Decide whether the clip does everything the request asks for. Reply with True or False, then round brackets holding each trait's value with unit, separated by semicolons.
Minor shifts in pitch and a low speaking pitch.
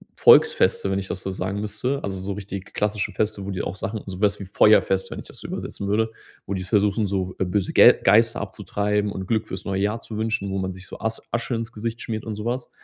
True (2.3 semitones; 105 Hz)